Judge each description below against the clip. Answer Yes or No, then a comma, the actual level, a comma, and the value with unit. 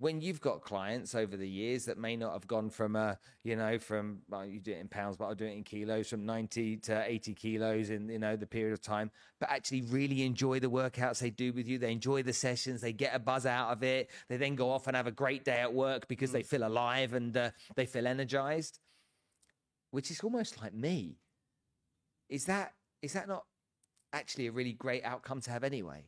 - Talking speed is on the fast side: Yes, fast, 230 wpm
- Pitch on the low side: Yes, low, 120 Hz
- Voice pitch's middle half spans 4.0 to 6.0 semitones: No, average, 3.3 semitones